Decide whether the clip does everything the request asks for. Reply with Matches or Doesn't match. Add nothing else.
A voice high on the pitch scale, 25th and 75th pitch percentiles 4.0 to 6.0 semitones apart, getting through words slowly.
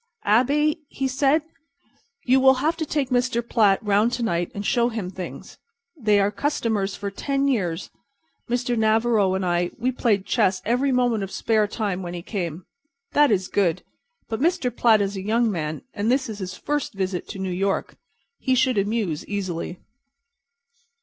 Doesn't match